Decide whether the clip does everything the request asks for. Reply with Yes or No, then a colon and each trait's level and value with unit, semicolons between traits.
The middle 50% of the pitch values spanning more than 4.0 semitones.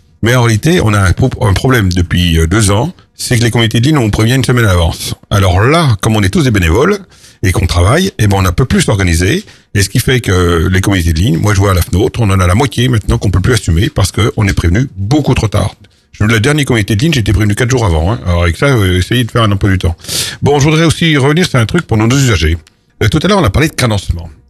Yes: average, 5.1 semitones